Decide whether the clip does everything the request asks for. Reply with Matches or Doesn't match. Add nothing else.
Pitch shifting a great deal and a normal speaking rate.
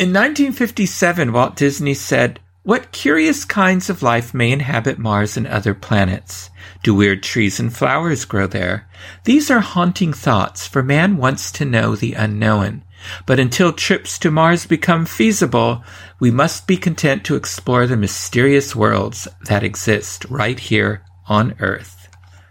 Matches